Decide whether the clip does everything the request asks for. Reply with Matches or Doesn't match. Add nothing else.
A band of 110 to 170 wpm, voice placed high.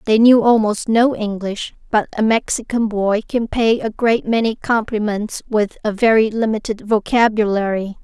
Matches